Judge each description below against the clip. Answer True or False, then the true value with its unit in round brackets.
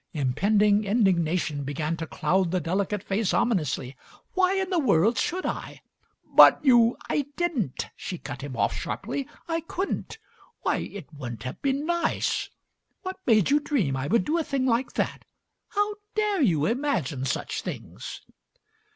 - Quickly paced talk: False (160 wpm)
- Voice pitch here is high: True (210 Hz)